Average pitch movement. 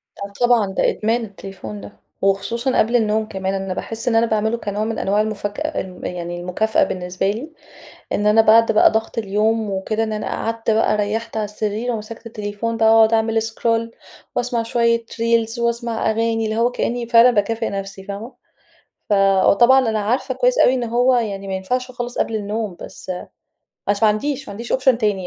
No: narrow, 2.2 semitones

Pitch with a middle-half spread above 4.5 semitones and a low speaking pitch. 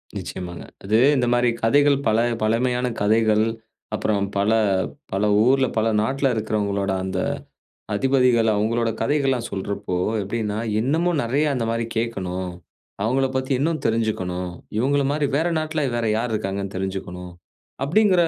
Yes: average, 4.9 semitones; low, 115 Hz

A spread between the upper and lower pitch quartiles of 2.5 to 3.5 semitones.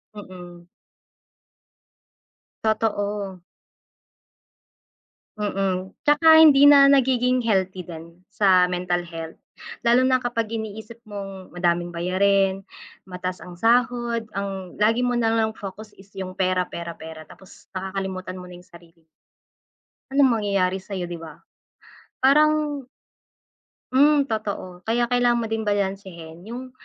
No: average, 4.5 semitones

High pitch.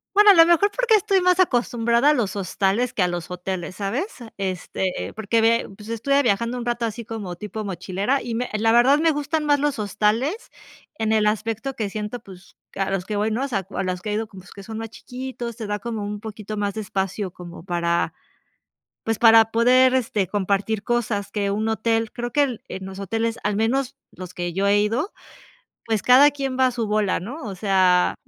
Yes: high, 220 Hz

